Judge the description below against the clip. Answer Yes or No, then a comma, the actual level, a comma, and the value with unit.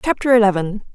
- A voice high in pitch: Yes, high, 215 Hz